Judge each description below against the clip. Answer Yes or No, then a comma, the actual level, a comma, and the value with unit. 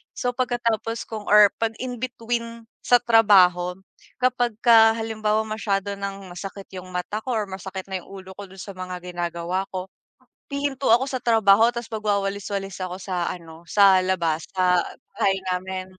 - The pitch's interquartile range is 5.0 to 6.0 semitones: No, average, 3.5 semitones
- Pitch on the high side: Yes, high, 200 Hz